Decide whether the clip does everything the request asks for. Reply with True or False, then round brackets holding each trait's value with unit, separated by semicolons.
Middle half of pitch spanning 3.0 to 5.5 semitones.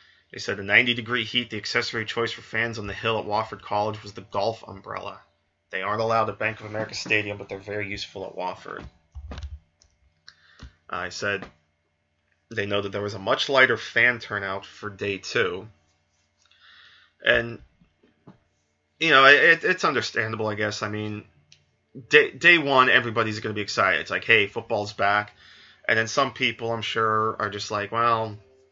False (2.6 semitones)